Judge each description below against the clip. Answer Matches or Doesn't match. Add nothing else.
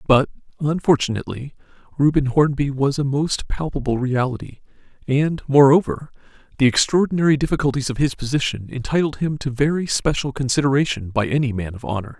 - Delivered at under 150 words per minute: Matches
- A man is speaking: Matches